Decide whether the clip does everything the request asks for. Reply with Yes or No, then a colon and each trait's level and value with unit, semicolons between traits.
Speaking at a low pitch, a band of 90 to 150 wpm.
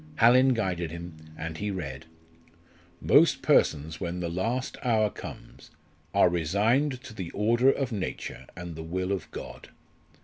Yes: very low, 95 Hz; average, 145 wpm